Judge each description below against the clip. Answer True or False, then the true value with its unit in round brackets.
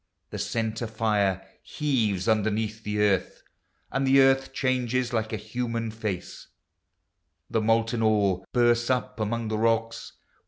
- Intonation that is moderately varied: False (1.9 semitones)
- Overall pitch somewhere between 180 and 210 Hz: False (110 Hz)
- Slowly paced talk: True (130 wpm)